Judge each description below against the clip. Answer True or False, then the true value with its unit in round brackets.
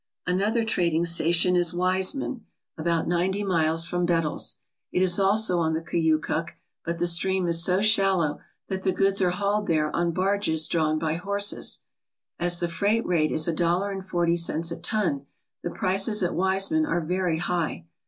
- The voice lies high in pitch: False (175 Hz)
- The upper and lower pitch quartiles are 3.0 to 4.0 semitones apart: False (2.5 semitones)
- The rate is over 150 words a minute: True (175 wpm)